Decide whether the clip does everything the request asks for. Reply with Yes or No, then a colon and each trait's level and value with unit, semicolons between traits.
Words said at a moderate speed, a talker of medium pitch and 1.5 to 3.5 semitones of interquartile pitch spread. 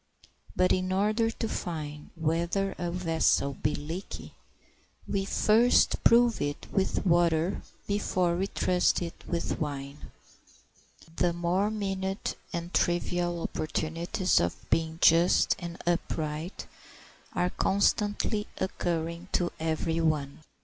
No: slow, 115 wpm; medium, 175 Hz; average, 2.9 semitones